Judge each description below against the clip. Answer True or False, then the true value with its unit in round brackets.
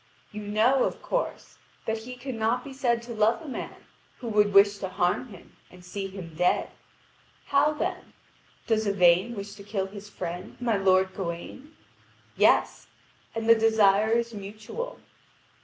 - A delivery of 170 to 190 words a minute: False (155 wpm)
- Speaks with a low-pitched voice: False (210 Hz)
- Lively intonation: False (3.4 semitones)